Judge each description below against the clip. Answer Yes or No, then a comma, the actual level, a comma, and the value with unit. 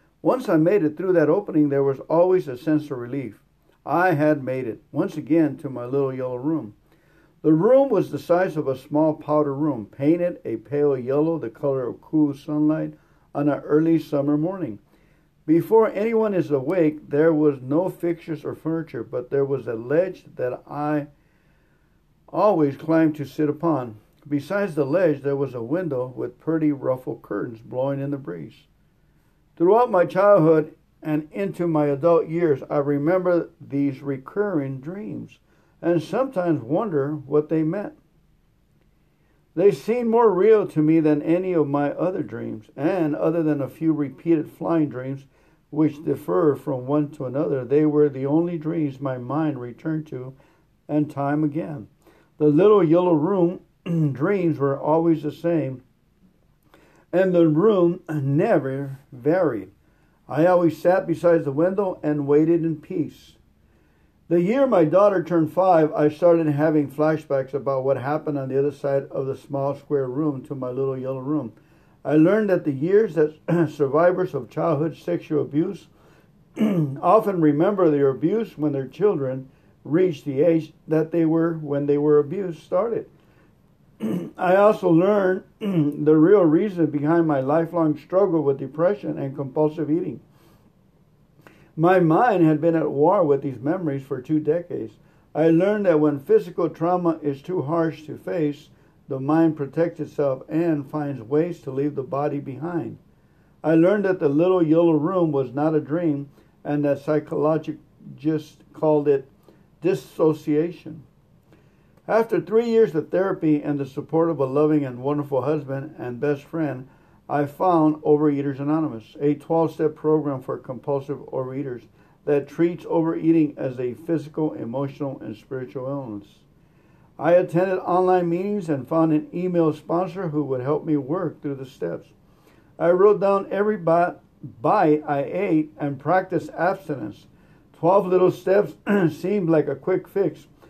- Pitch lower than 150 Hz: No, medium, 155 Hz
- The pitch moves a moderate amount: Yes, average, 3.0 semitones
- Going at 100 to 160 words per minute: Yes, average, 155 wpm